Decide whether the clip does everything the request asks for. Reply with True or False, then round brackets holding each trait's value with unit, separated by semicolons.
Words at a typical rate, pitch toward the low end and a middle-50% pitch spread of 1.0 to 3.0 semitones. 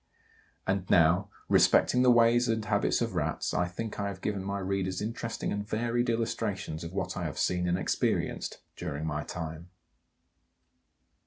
False (160 wpm; 100 Hz; 4.2 semitones)